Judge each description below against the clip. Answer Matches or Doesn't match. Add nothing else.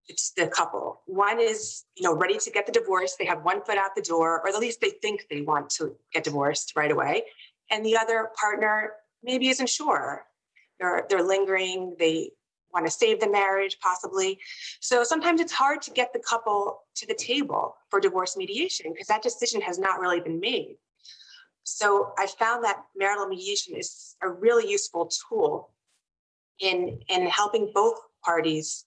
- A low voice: Doesn't match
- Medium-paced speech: Matches